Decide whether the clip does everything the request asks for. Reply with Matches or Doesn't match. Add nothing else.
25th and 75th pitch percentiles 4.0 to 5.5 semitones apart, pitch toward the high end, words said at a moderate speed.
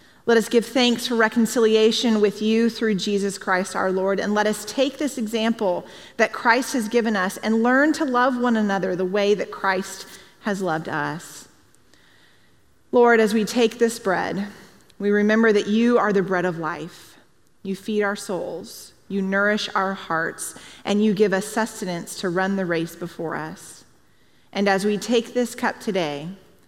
Doesn't match